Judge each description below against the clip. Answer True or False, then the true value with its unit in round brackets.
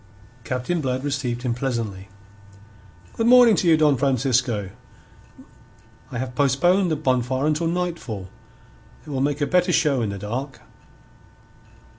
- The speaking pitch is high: False (135 Hz)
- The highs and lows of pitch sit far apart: False (4.2 semitones)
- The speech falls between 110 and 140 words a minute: True (135 wpm)